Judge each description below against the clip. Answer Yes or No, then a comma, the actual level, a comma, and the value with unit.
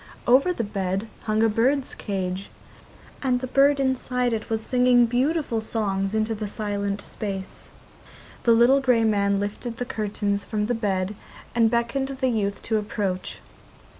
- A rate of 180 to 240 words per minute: No, average, 155 wpm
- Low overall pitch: No, high, 225 Hz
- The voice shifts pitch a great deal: No, average, 3.5 semitones